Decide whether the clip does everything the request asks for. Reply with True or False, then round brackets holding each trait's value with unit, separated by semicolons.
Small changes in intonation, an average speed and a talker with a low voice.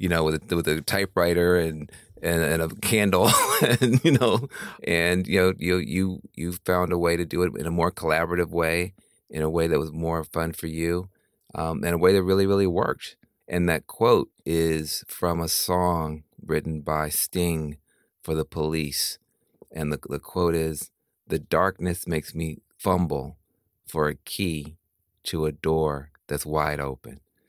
True (2.2 semitones; 175 wpm; 85 Hz)